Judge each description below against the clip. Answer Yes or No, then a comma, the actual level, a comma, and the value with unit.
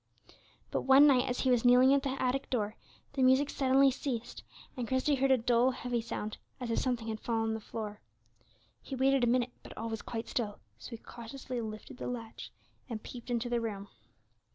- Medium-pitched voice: No, high, 245 Hz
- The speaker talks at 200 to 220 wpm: Yes, fast, 205 wpm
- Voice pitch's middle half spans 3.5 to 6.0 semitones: No, narrow, 2.5 semitones